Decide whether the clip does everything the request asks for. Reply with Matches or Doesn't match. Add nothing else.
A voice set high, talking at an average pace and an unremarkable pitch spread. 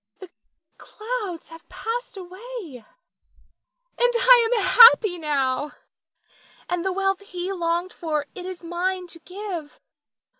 Doesn't match